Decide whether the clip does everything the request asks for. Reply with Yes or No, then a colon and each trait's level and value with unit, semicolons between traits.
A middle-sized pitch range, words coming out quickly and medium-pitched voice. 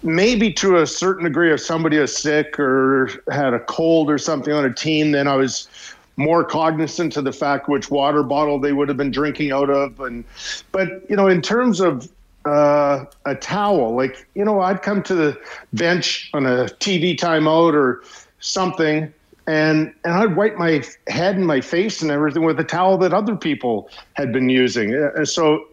No: average, 3.8 semitones; average, 190 wpm; medium, 155 Hz